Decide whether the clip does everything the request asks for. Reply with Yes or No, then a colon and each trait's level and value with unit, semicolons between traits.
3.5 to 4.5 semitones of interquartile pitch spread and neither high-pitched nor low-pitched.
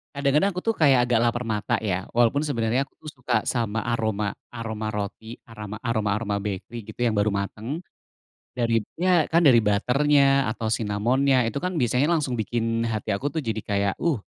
No: average, 4.2 semitones; low, 115 Hz